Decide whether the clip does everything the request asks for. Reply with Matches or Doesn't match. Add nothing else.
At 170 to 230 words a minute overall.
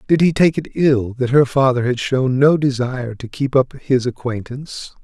Matches